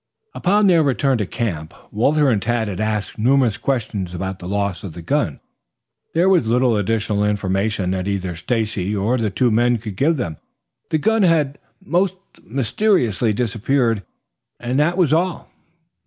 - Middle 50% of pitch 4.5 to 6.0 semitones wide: Yes, wide, 5.6 semitones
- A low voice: Yes, low, 115 Hz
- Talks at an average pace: Yes, average, 155 wpm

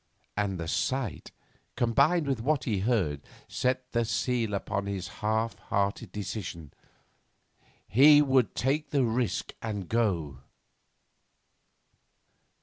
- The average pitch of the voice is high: No, low, 110 Hz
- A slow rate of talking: Yes, slow, 110 wpm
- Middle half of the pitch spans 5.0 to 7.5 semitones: No, average, 4.4 semitones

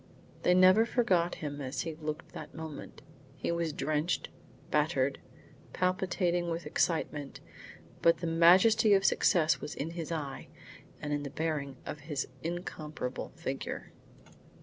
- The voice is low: No, medium, 165 Hz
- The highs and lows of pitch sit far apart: No, average, 2.9 semitones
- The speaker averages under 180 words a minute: Yes, average, 140 wpm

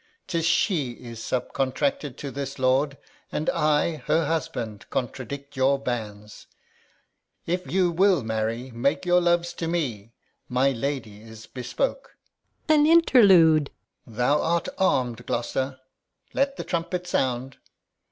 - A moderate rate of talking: No, slow, 130 wpm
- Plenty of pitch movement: Yes, wide, 5.7 semitones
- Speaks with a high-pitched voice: No, medium, 140 Hz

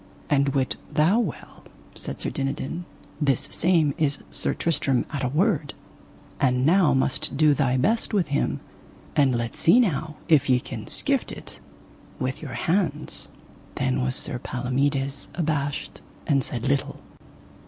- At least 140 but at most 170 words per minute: Yes, average, 150 wpm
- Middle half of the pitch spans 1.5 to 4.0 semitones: Yes, average, 3.2 semitones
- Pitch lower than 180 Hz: Yes, medium, 140 Hz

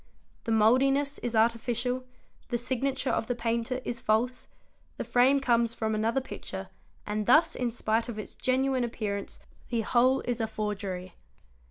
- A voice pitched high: Yes, high, 235 Hz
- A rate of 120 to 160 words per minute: Yes, average, 155 wpm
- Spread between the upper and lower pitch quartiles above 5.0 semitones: No, narrow, 2.6 semitones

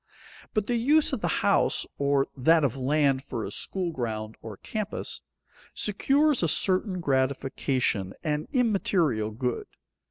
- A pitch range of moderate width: No, wide, 7.5 semitones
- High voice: No, medium, 145 Hz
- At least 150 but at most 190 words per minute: No, slow, 135 wpm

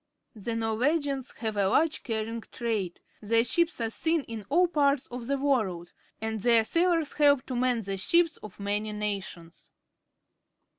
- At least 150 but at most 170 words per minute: Yes, average, 155 wpm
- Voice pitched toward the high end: Yes, high, 230 Hz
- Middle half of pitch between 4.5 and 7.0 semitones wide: Yes, average, 5.1 semitones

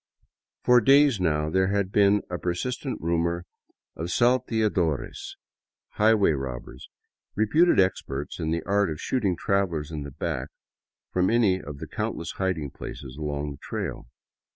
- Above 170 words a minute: No, average, 140 wpm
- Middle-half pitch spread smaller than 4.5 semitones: No, wide, 5.4 semitones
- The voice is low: Yes, very low, 90 Hz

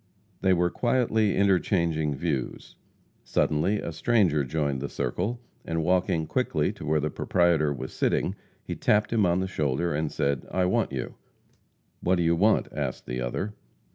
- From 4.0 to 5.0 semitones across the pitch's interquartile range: Yes, average, 4.3 semitones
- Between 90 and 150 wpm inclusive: No, average, 165 wpm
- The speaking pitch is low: Yes, very low, 85 Hz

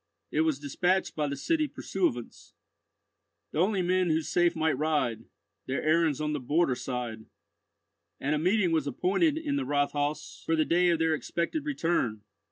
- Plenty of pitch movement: No, average, 3.9 semitones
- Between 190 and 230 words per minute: No, average, 170 wpm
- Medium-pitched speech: Yes, medium, 160 Hz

